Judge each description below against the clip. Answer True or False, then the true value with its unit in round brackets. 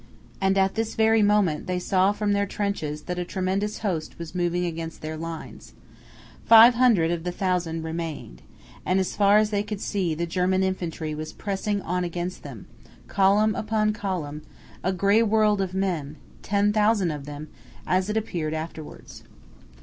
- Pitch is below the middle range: False (185 Hz)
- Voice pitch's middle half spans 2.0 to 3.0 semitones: False (3.8 semitones)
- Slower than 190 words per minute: True (170 wpm)